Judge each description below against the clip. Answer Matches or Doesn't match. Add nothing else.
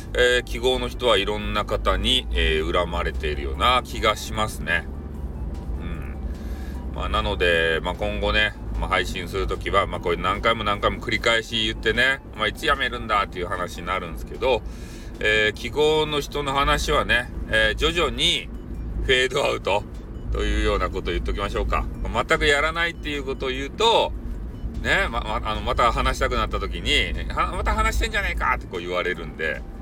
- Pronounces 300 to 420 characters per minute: Matches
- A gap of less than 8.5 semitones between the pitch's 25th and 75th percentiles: Matches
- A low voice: Matches